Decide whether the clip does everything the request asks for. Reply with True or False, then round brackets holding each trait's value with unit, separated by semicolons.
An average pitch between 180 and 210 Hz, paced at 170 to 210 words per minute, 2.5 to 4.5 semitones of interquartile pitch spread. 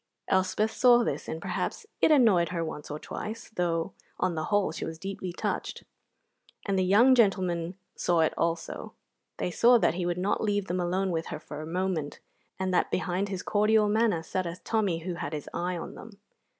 True (185 Hz; 200 wpm; 3.4 semitones)